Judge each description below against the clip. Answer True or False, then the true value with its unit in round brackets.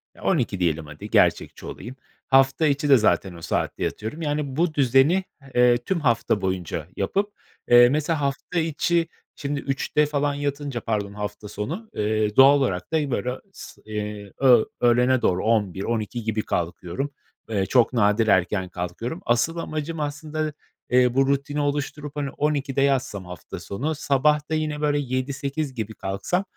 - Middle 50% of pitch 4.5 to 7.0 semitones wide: True (5.6 semitones)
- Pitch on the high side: False (130 Hz)